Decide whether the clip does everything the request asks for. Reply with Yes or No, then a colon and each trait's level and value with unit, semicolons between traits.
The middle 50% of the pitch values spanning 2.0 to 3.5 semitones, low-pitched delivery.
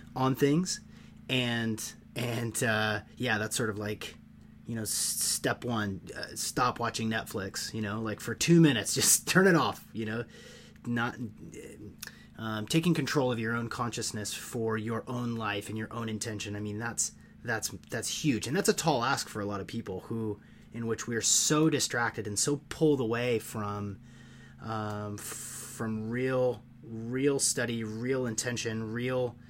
Yes: narrow, 2.5 semitones; low, 115 Hz